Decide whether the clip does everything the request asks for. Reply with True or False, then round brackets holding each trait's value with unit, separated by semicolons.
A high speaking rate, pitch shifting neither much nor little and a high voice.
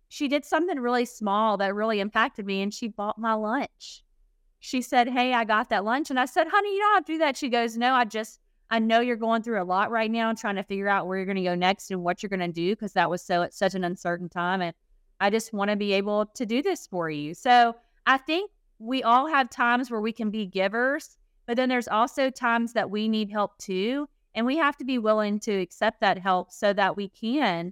True (260 wpm; 4.0 semitones; 220 Hz)